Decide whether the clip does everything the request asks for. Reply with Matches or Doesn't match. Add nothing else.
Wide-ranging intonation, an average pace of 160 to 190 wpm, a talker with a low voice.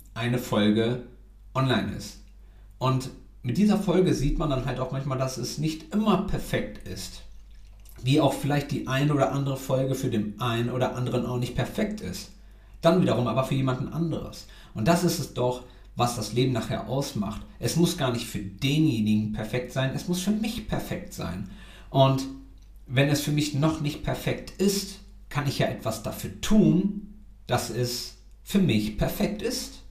Matches